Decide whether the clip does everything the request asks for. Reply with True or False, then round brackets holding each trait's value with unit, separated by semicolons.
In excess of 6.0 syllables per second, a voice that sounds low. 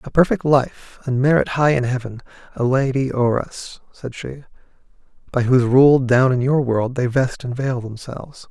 False (4.8 syllables/s; 130 Hz)